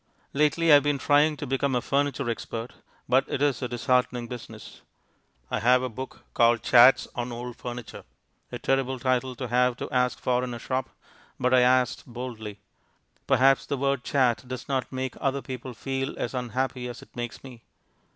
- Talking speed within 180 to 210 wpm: Yes, average, 185 wpm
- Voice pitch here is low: Yes, low, 125 Hz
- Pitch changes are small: Yes, narrow, 1.6 semitones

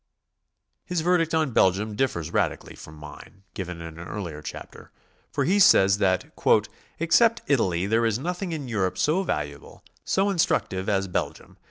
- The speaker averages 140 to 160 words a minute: Yes, average, 155 wpm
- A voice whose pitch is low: Yes, low, 105 Hz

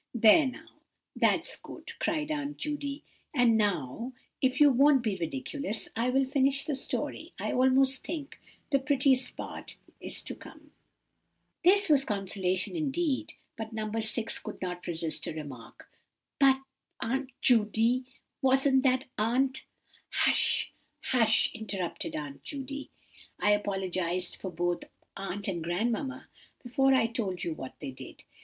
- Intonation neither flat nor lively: No, wide, 5.7 semitones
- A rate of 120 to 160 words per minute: Yes, slow, 135 wpm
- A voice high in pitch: Yes, high, 245 Hz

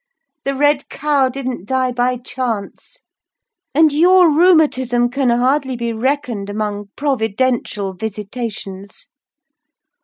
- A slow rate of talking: Yes, slow, 100 wpm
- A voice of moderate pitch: No, very high, 250 Hz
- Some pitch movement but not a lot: Yes, average, 4.3 semitones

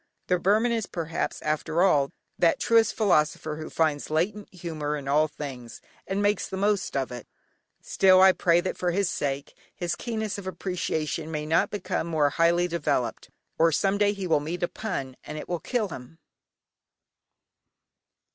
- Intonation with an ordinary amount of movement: Yes, average, 4.1 semitones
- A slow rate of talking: No, average, 170 wpm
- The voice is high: No, medium, 170 Hz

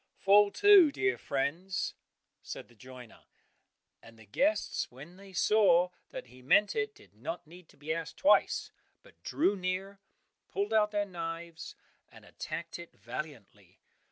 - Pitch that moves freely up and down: Yes, wide, 6.1 semitones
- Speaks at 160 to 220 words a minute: No, average, 150 wpm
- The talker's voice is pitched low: No, medium, 175 Hz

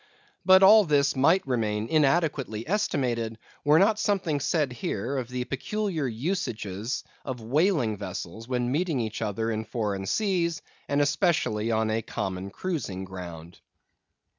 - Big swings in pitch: Yes, wide, 6.9 semitones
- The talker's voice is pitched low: Yes, low, 125 Hz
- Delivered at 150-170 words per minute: No, average, 140 wpm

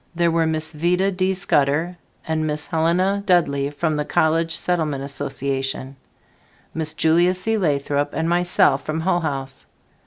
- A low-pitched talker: No, medium, 160 Hz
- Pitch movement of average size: Yes, average, 3.4 semitones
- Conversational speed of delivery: Yes, average, 145 wpm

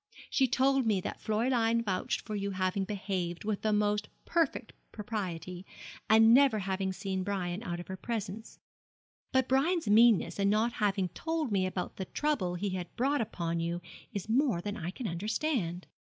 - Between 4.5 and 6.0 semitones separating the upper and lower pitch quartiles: No, average, 3.9 semitones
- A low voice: No, high, 205 Hz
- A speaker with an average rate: Yes, average, 170 wpm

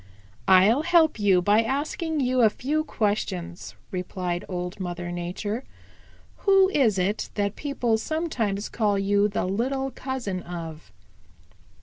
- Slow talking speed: Yes, slow, 125 wpm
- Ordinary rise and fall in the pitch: No, wide, 6.5 semitones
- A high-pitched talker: Yes, high, 210 Hz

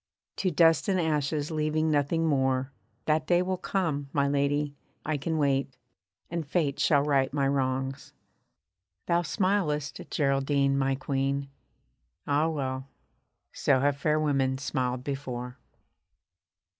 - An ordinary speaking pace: No, slow, 125 wpm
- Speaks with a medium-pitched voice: Yes, medium, 145 Hz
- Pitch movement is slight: Yes, narrow, 2.3 semitones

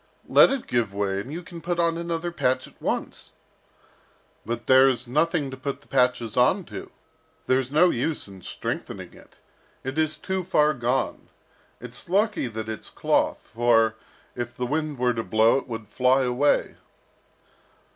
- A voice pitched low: Yes, low, 130 Hz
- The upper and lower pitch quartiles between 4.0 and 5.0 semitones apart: Yes, average, 4.7 semitones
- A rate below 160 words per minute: No, average, 165 wpm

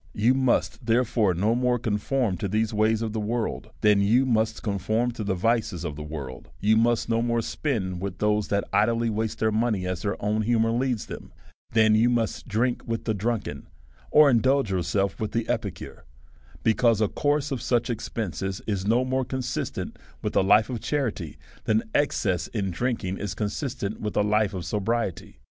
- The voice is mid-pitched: No, low, 110 Hz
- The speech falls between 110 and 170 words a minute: No, average, 190 wpm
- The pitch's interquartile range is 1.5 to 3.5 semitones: Yes, average, 2.9 semitones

